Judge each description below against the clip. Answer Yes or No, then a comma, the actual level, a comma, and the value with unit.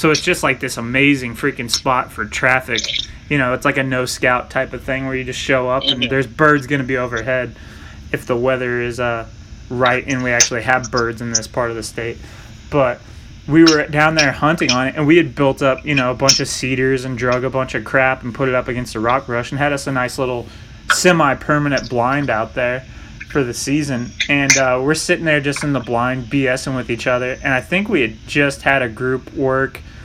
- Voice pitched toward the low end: Yes, low, 130 Hz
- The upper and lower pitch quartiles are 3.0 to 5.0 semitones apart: No, narrow, 2.4 semitones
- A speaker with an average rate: No, fast, 240 wpm